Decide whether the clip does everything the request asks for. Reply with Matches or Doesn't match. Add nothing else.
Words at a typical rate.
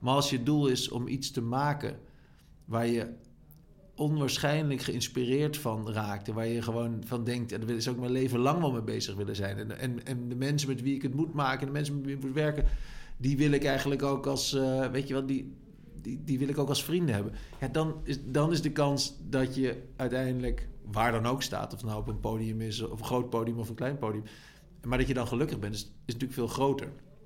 Doesn't match